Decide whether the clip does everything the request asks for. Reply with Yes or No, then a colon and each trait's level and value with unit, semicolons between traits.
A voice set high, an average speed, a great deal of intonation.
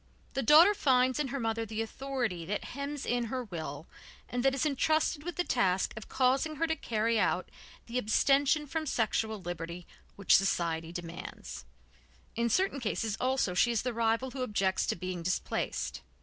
Yes: high, 235 Hz; average, 175 wpm; wide, 5.8 semitones